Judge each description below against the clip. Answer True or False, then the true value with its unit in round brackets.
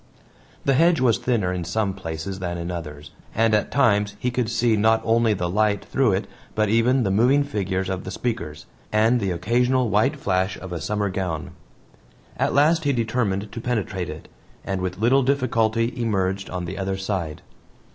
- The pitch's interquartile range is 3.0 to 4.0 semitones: False (4.4 semitones)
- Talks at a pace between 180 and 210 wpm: True (185 wpm)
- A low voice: True (105 Hz)